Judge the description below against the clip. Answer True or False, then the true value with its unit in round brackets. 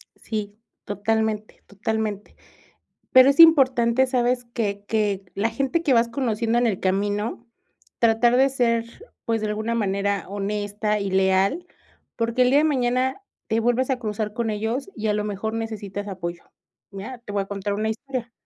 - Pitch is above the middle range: True (220 Hz)